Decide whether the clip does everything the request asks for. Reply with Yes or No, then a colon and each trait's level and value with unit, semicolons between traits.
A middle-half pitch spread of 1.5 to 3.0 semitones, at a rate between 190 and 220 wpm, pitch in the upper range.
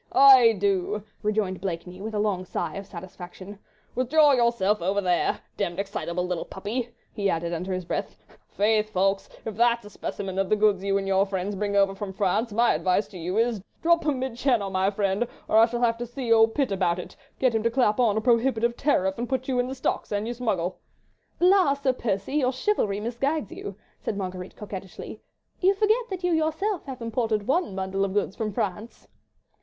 No: average, 4.1 semitones; fast, 205 wpm; high, 210 Hz